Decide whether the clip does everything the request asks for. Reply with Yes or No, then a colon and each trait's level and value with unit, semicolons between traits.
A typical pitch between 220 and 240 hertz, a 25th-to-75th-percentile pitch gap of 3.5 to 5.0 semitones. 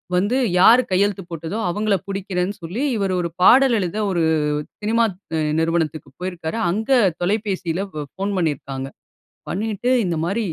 No: high, 190 Hz; average, 3.8 semitones